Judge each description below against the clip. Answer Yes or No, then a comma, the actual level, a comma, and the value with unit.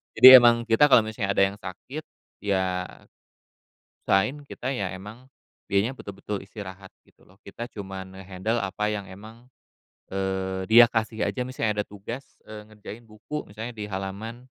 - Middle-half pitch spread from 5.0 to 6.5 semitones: No, average, 3.2 semitones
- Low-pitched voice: Yes, low, 105 Hz